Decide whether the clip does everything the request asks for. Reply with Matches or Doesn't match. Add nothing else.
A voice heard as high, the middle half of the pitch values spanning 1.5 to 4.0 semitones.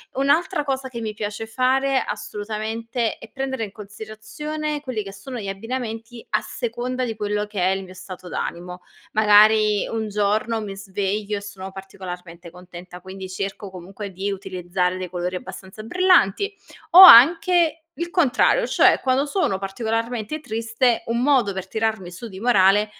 Doesn't match